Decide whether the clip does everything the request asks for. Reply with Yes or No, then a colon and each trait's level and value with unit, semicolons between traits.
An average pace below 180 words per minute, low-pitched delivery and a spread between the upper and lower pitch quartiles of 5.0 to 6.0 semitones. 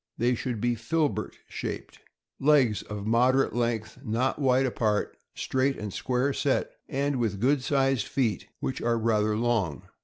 No: average, 155 wpm; low, 120 Hz; average, 3.5 semitones